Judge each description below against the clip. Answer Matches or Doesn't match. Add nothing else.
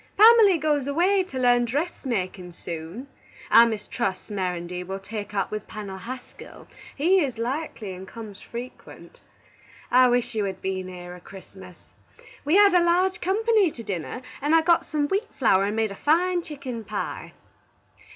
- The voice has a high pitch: Matches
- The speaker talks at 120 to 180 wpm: Matches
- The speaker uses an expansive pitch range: Matches